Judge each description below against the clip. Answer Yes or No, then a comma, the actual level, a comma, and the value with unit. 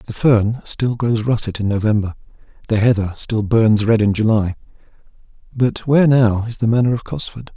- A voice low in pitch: Yes, low, 110 Hz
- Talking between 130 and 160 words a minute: No, average, 175 wpm